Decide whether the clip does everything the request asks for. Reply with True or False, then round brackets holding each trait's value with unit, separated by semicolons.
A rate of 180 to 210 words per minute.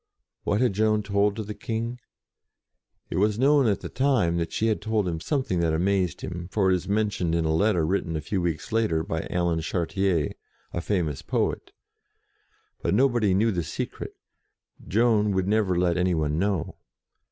True (185 wpm)